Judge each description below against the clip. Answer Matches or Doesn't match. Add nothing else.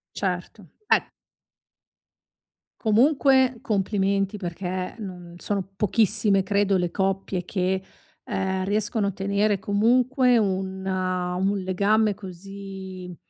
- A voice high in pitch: Matches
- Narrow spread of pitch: Matches